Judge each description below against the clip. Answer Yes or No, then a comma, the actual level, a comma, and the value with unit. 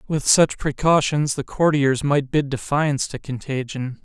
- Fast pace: No, average, 150 wpm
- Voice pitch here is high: No, medium, 140 Hz